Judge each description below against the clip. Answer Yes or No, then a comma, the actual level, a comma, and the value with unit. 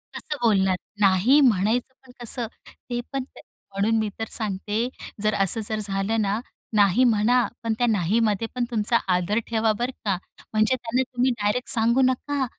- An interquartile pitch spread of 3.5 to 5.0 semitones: No, average, 3.0 semitones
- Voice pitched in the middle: No, high, 225 Hz